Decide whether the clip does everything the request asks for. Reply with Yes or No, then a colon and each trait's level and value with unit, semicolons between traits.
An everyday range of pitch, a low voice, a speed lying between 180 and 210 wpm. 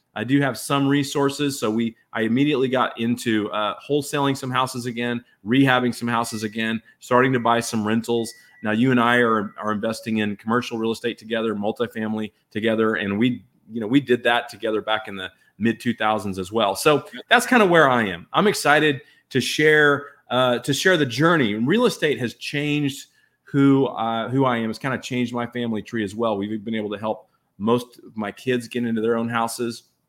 Yes: average, 3.4 semitones; low, 120 Hz; fast, 205 wpm